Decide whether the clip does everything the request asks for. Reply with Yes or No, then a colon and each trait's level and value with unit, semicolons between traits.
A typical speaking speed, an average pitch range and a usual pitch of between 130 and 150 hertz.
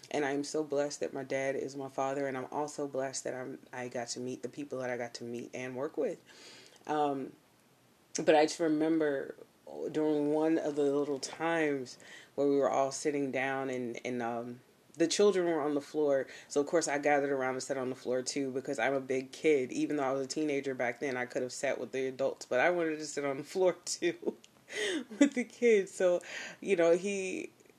No: fast, 225 wpm; average, 3.5 semitones; medium, 140 Hz